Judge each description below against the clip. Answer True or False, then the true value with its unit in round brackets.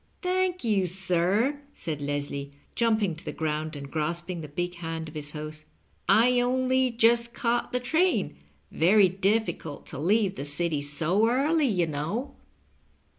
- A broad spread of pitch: True (7.4 semitones)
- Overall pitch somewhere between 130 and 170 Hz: False (185 Hz)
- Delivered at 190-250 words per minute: False (160 wpm)